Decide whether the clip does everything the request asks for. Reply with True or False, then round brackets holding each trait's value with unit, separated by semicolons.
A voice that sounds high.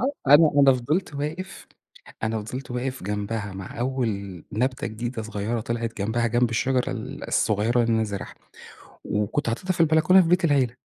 False (120 Hz)